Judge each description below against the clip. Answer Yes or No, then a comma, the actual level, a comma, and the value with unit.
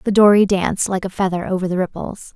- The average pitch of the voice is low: No, high, 190 Hz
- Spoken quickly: Yes, fast, 230 wpm